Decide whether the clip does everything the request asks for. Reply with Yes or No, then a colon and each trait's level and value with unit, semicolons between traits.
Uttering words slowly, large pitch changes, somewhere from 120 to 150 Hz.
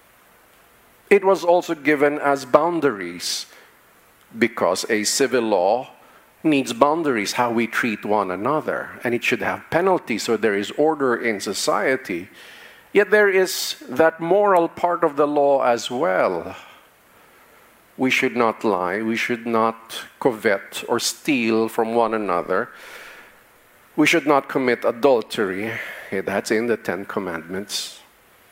Yes: slow, 130 wpm; wide, 6.3 semitones; medium, 140 Hz